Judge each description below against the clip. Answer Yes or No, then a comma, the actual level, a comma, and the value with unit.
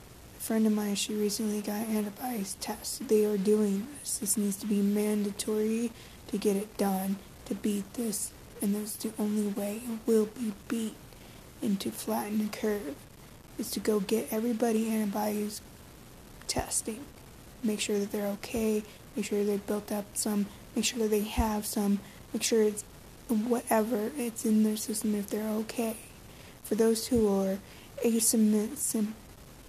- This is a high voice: Yes, high, 215 Hz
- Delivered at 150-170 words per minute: Yes, average, 160 wpm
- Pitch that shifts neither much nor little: No, narrow, 1.3 semitones